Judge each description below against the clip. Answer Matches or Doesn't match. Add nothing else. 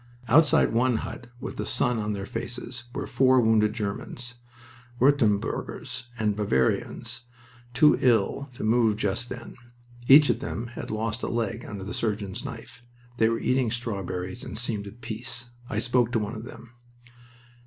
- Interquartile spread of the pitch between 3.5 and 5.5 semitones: Doesn't match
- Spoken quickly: Doesn't match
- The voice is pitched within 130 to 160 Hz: Doesn't match